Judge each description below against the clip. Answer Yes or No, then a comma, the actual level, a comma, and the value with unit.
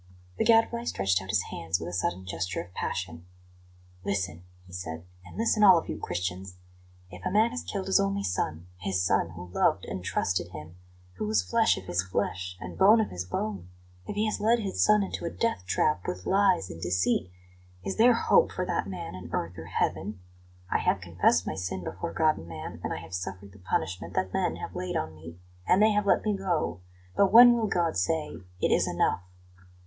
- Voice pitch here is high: No, very low, 95 Hz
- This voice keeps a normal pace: No, fast, 215 wpm